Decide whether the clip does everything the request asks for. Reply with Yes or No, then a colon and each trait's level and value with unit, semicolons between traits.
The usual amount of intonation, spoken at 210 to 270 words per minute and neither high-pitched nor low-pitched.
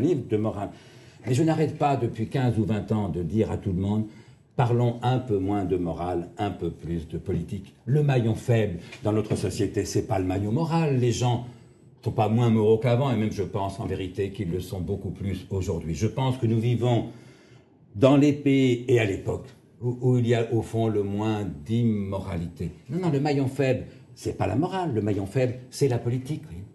No: average, 4.2 semitones; fast, 220 wpm; low, 110 Hz